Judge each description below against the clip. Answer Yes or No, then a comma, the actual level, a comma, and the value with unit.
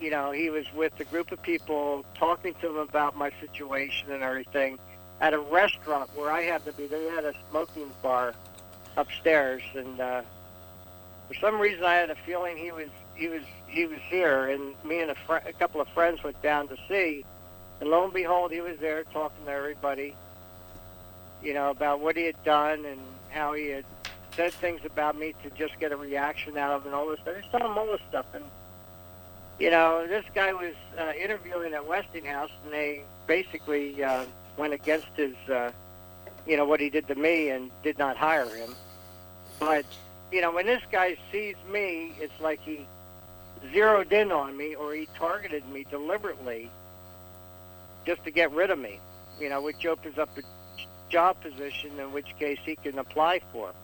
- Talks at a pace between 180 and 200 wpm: Yes, average, 190 wpm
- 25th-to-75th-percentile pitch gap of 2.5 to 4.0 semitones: No, average, 4.8 semitones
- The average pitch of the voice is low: No, medium, 145 Hz